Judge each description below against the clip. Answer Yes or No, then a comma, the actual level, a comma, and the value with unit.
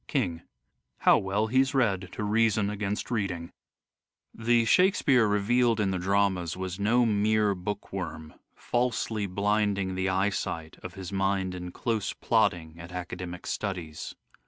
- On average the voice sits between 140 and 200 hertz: No, low, 100 Hz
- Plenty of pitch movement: No, average, 3.1 semitones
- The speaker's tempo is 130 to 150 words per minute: Yes, average, 145 wpm